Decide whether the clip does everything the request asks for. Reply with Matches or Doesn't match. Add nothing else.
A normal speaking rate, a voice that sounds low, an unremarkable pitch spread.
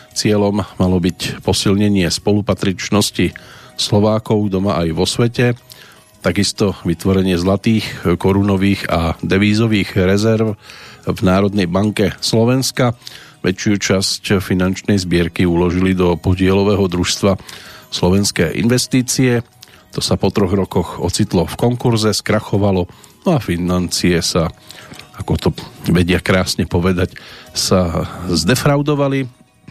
Doesn't match